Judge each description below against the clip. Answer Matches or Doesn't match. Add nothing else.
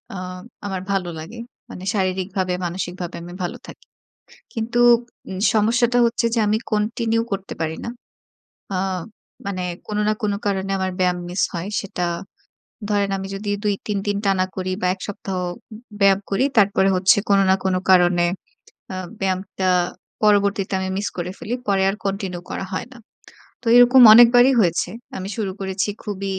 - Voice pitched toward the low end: Doesn't match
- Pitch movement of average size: Doesn't match